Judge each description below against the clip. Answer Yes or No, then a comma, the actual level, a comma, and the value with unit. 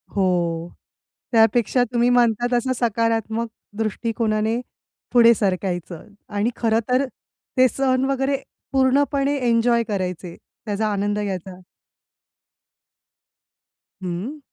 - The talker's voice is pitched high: Yes, high, 225 Hz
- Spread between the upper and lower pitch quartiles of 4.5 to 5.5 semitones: No, average, 3.6 semitones